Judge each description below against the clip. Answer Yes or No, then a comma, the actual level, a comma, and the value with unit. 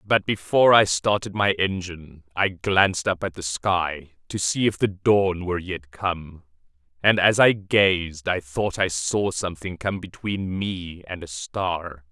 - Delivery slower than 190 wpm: Yes, average, 175 wpm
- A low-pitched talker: Yes, very low, 90 Hz